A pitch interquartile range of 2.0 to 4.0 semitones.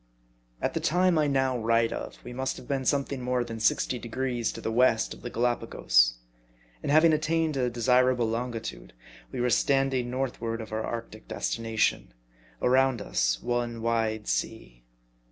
Yes: average, 2.7 semitones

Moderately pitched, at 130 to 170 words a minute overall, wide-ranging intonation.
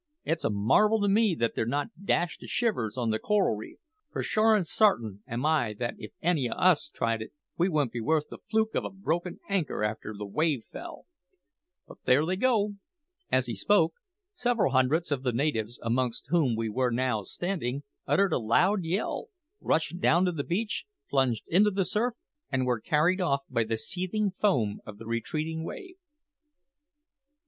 No: medium, 155 Hz; average, 185 wpm; wide, 8.2 semitones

